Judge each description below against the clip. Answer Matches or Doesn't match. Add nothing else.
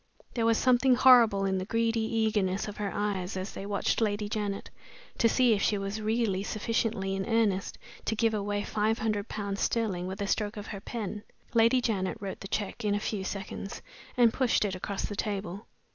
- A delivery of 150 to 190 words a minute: Doesn't match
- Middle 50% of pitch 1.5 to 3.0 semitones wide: Matches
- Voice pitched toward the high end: Matches